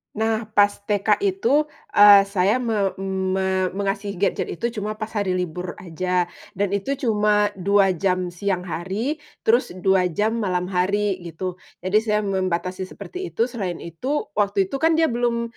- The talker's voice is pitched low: No, high, 200 Hz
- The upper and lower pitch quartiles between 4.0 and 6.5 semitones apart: No, average, 2.9 semitones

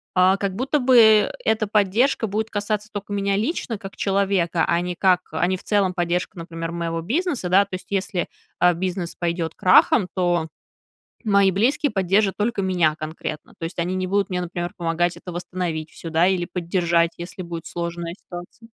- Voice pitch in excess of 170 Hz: Yes, medium, 185 Hz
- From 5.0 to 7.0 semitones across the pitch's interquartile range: No, average, 2.9 semitones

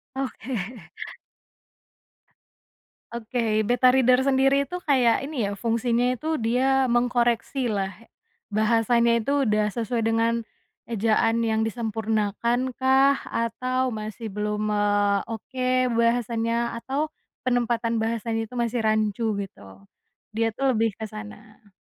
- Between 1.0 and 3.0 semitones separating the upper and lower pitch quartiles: Yes, narrow, 2.5 semitones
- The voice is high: Yes, high, 230 Hz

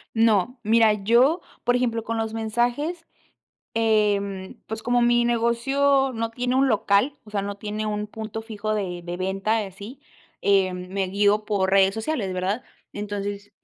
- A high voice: Yes, high, 215 Hz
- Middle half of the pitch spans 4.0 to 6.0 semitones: No, average, 2.9 semitones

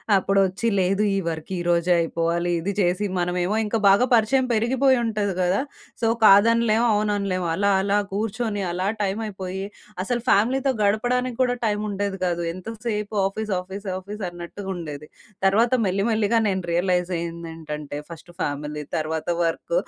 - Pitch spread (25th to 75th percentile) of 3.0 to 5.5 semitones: Yes, average, 3.7 semitones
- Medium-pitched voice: No, high, 195 Hz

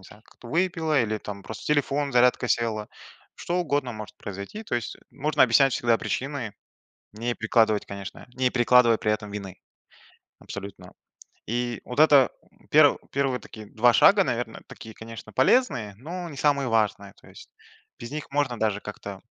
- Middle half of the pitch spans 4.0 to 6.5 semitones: Yes, average, 4.5 semitones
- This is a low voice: Yes, low, 120 Hz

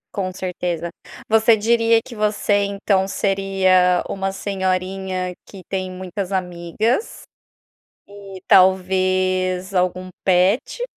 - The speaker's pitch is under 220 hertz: Yes, high, 190 Hz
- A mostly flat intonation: Yes, narrow, 1.5 semitones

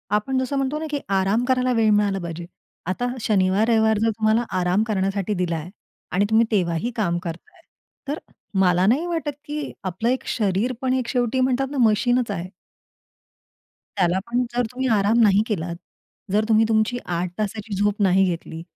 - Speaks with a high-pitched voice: Yes, high, 215 Hz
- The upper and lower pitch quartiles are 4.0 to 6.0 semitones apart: Yes, average, 4.5 semitones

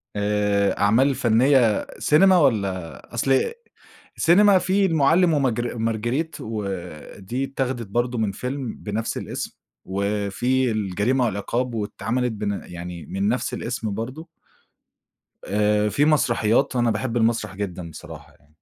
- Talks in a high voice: No, low, 115 Hz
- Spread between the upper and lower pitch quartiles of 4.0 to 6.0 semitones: Yes, average, 4.4 semitones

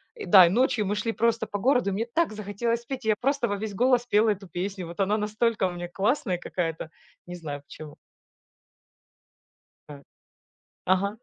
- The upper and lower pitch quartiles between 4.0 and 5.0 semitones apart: Yes, average, 4.3 semitones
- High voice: Yes, high, 210 Hz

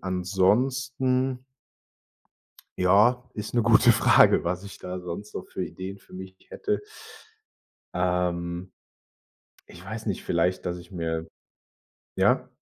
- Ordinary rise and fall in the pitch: Yes, average, 4.5 semitones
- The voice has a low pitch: Yes, very low, 95 Hz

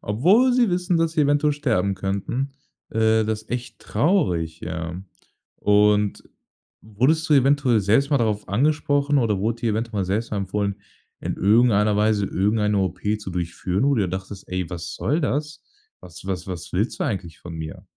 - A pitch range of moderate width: No, wide, 6.4 semitones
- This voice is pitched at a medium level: No, low, 105 Hz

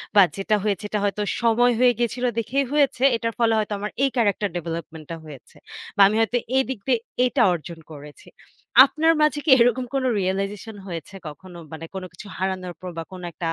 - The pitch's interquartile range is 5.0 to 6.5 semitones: Yes, wide, 5.4 semitones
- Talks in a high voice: Yes, high, 210 Hz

